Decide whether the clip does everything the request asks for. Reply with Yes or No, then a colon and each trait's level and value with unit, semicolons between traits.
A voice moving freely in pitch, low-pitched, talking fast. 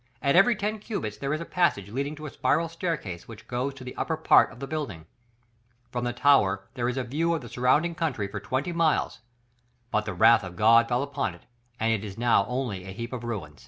Yes: wide, 5.9 semitones; low, 125 Hz; fast, 235 wpm